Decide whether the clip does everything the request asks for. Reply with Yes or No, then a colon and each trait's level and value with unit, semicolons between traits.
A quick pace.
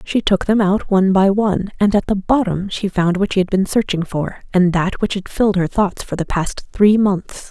Yes: fast, 250 wpm